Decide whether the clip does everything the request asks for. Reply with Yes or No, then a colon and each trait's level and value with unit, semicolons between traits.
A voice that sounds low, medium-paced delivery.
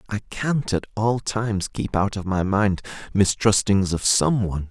Yes: low, 100 Hz; average, 180 wpm